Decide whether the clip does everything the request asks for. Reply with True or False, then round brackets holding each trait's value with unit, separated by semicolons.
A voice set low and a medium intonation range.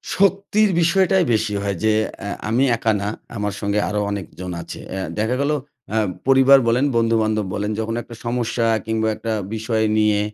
True (110 Hz; 3.8 semitones)